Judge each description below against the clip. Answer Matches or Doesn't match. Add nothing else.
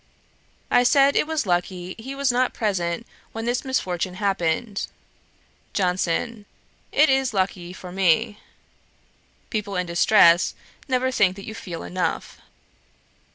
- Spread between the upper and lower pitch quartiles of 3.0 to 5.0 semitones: Doesn't match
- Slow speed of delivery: Matches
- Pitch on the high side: Matches